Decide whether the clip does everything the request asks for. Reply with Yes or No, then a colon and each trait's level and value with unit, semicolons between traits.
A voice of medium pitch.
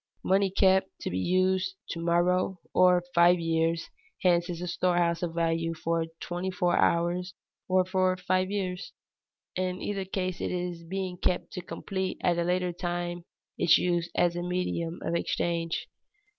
Yes: medium, 180 Hz